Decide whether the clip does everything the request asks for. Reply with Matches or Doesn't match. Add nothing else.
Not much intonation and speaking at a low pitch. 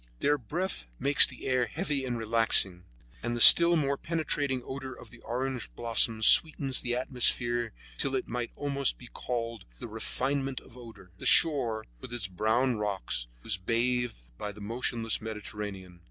Doesn't match